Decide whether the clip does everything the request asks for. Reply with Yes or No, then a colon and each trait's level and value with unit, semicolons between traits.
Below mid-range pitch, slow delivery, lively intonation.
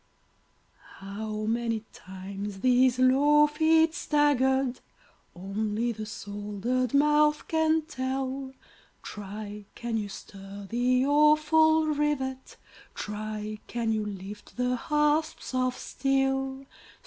No: very high, 255 Hz; slow, 100 wpm; wide, 5.7 semitones